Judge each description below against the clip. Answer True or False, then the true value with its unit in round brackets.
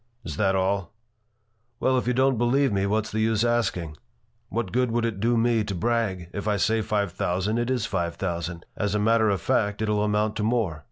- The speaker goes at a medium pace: False (220 wpm)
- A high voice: False (105 Hz)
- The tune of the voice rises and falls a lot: False (3.1 semitones)